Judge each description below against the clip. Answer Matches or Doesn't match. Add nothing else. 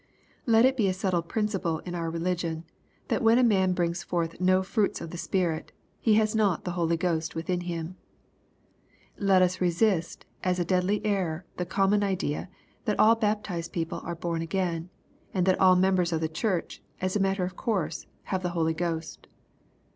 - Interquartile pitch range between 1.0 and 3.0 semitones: Matches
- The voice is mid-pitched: Matches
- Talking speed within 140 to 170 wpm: Doesn't match